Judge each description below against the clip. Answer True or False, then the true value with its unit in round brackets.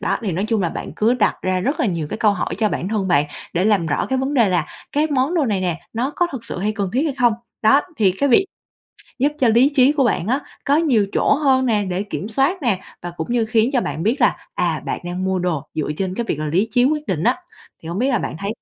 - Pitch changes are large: True (6.1 semitones)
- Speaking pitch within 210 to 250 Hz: True (220 Hz)